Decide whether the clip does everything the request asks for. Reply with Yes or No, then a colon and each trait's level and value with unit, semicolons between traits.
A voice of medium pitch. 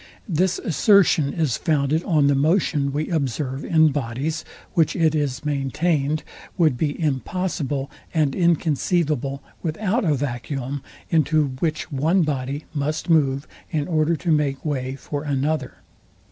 Yes: medium, 150 Hz